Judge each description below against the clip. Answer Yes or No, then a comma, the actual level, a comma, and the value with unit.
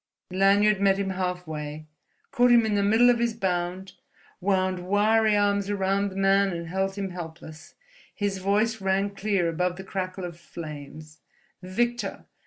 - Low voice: No, high, 195 Hz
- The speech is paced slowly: No, average, 155 wpm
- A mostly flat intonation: Yes, narrow, 2.2 semitones